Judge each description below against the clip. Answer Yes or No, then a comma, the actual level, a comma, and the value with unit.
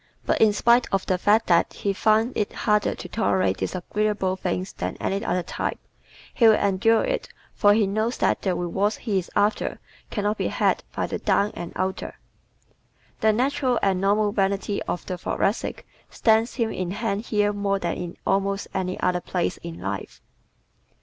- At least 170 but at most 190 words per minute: Yes, average, 180 wpm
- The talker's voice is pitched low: No, high, 200 Hz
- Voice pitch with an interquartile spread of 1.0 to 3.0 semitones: Yes, average, 2.7 semitones